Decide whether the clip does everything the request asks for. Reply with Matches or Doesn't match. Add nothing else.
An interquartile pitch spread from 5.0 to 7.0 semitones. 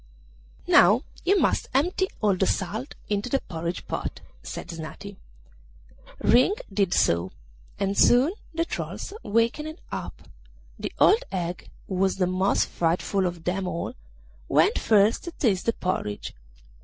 Matches